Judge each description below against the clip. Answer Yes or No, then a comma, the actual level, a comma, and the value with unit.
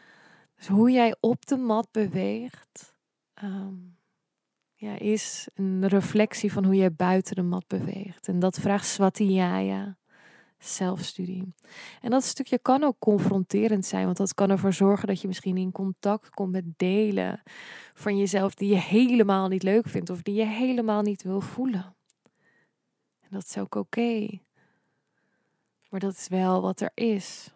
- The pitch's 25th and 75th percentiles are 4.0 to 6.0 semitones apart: No, narrow, 2.4 semitones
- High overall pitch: Yes, high, 195 Hz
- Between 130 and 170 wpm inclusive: Yes, average, 155 wpm